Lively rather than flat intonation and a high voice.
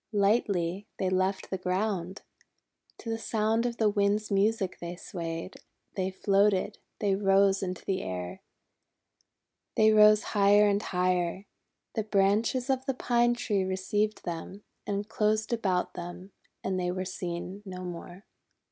No: narrow, 2.6 semitones; high, 195 Hz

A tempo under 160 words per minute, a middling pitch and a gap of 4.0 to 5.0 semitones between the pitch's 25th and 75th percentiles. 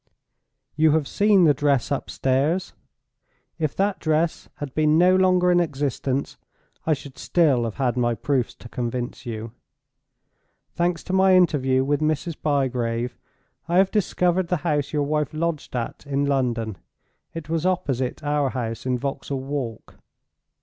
Yes: average, 150 wpm; medium, 145 Hz; average, 4.6 semitones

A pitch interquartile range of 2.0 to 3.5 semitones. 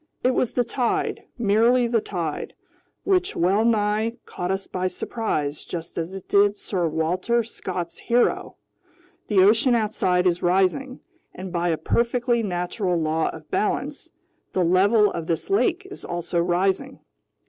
No: average, 5.1 semitones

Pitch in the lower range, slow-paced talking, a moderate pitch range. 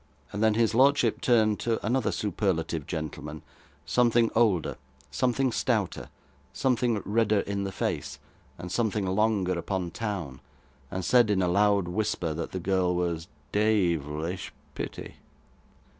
Yes: low, 100 Hz; slow, 130 wpm; average, 4.2 semitones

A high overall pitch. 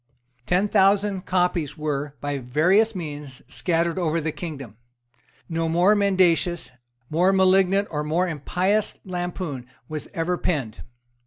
No: medium, 170 Hz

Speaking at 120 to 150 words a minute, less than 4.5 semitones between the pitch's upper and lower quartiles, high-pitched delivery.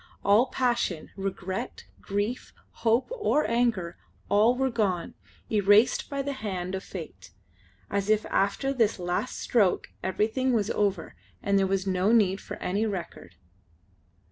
Yes: average, 140 wpm; average, 3.6 semitones; high, 205 Hz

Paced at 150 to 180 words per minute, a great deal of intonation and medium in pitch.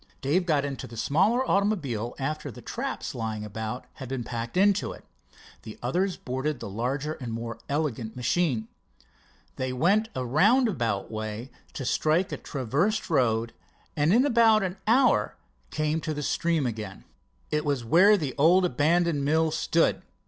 Yes: average, 155 wpm; wide, 6.7 semitones; medium, 145 Hz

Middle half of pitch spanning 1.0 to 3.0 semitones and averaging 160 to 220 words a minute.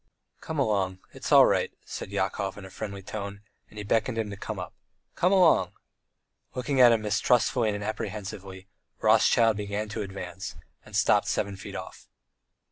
Yes: narrow, 2.5 semitones; average, 165 wpm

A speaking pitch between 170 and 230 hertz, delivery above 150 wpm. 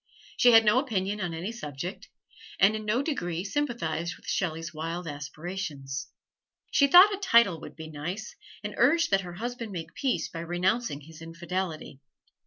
Yes: medium, 185 Hz; average, 165 wpm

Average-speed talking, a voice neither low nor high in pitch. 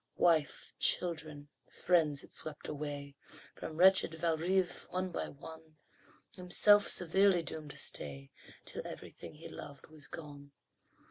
No: slow, 125 wpm; medium, 160 Hz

